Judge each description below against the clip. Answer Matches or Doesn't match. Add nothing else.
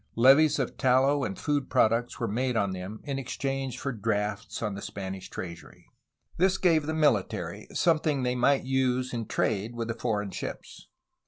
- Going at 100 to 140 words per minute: Doesn't match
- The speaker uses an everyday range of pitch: Matches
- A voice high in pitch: Doesn't match